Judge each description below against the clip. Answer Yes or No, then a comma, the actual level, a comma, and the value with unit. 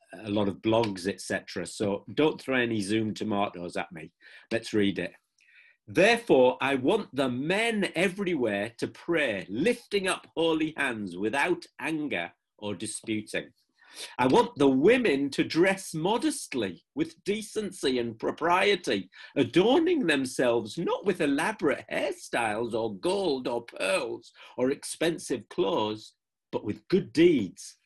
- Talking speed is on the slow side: Yes, slow, 130 wpm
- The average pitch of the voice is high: No, low, 135 Hz